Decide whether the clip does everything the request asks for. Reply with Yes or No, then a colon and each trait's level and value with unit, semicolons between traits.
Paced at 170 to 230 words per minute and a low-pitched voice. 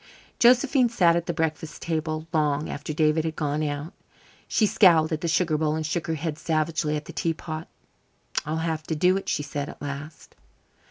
No: average, 200 wpm; medium, 155 Hz